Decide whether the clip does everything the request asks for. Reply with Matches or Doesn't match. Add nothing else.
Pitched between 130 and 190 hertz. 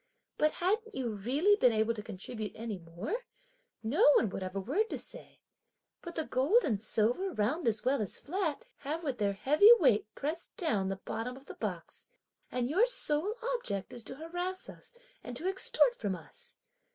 Doesn't match